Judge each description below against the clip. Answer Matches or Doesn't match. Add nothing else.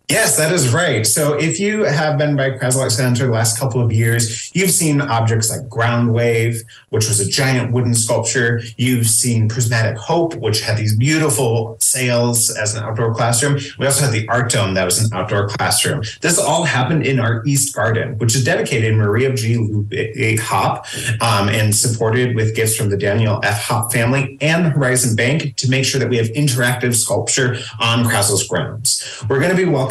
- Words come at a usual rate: Matches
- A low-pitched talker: Matches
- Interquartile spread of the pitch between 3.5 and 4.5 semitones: Doesn't match